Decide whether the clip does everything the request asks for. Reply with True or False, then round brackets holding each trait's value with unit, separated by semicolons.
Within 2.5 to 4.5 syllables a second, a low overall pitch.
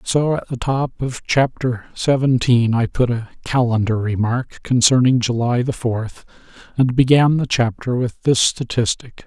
True (4.3 syllables/s; 125 Hz)